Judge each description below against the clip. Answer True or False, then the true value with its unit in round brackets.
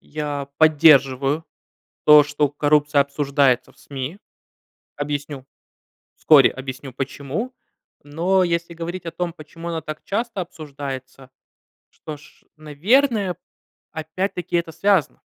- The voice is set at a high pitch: False (150 Hz)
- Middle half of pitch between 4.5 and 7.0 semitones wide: False (3.3 semitones)